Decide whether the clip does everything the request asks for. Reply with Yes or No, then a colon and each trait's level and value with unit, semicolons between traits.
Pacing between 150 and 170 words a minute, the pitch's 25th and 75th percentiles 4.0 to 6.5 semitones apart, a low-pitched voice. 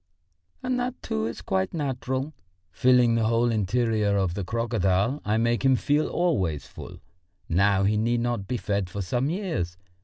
Yes: average, 165 wpm; average, 4.6 semitones; low, 115 Hz